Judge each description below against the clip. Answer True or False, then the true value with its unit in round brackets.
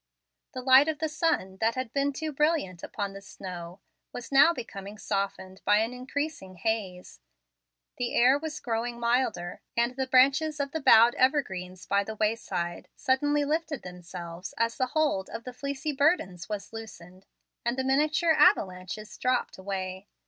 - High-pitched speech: True (235 Hz)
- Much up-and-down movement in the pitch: True (6.5 semitones)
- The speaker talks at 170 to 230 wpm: False (155 wpm)